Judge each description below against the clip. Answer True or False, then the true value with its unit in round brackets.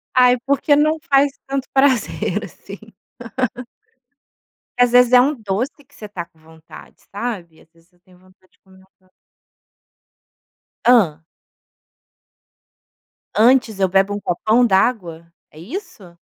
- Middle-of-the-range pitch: False (210 Hz)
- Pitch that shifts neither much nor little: False (5.9 semitones)